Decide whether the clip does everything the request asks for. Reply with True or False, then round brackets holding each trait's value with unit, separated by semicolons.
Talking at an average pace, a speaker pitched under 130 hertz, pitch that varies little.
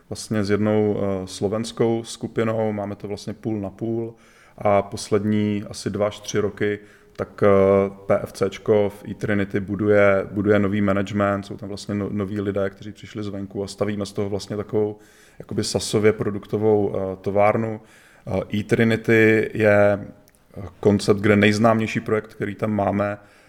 True (155 wpm; 105 Hz; 1.2 semitones)